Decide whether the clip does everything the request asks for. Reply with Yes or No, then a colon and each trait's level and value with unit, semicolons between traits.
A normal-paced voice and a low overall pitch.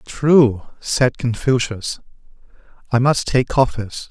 No: slow, 100 wpm; low, 125 Hz